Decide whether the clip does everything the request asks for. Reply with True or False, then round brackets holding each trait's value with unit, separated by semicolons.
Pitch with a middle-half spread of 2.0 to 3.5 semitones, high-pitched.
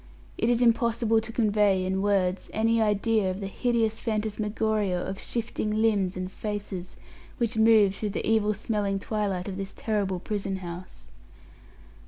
True (2.4 semitones; 210 Hz)